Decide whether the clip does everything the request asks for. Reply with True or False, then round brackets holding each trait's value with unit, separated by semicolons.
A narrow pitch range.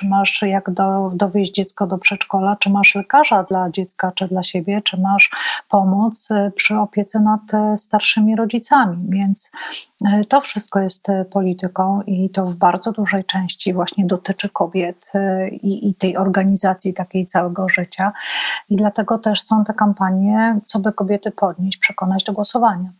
True (1.9 semitones)